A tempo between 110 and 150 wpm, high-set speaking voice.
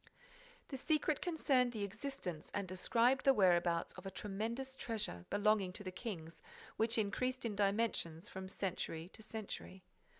Yes: average, 145 wpm; high, 210 Hz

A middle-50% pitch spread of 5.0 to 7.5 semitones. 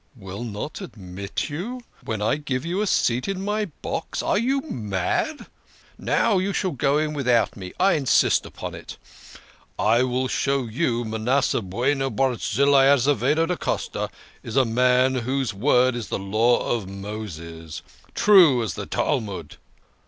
Yes: wide, 5.4 semitones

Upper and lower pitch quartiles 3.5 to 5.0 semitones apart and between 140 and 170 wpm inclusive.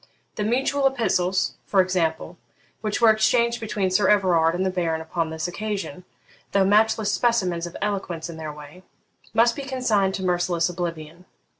Yes: average, 4.1 semitones; average, 160 wpm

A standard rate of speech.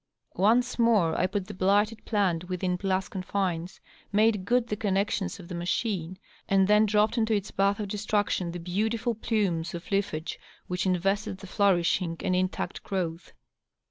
Yes: average, 160 wpm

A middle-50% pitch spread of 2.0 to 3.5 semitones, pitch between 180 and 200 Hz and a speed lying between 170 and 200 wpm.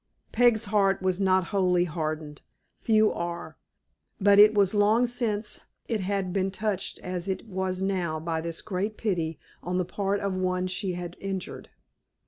No: narrow, 2.4 semitones; high, 190 Hz; average, 160 wpm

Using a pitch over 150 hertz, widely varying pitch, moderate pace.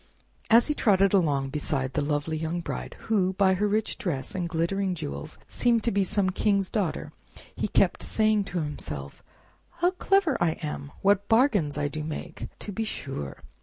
Yes: medium, 185 Hz; wide, 5.9 semitones; average, 175 wpm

